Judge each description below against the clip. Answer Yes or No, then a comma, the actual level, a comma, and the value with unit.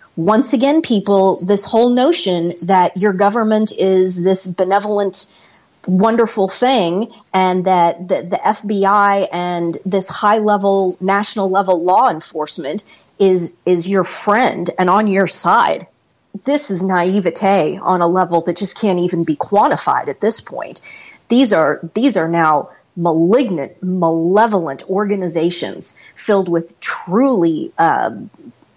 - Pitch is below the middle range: No, high, 195 Hz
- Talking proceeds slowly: Yes, slow, 130 wpm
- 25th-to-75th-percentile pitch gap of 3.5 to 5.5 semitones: No, average, 2.9 semitones